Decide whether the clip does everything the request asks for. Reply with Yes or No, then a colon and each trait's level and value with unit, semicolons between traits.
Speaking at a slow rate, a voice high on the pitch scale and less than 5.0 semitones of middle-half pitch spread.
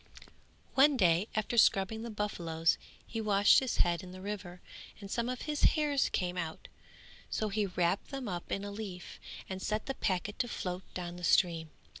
No: average, 185 wpm; high, 200 Hz; average, 3.7 semitones